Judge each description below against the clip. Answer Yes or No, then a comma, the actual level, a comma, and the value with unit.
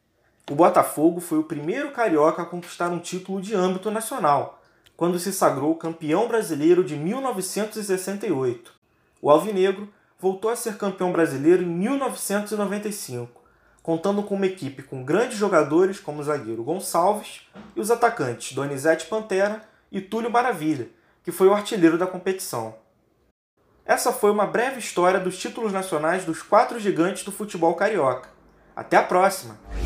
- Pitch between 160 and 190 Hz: Yes, medium, 185 Hz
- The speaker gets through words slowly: No, average, 145 wpm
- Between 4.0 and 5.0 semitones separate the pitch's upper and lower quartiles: Yes, average, 4.4 semitones